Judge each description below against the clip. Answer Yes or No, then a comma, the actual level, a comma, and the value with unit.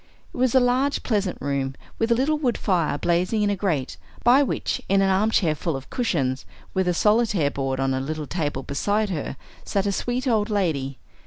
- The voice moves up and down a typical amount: No, wide, 7.8 semitones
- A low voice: No, high, 190 Hz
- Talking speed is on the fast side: Yes, fast, 210 wpm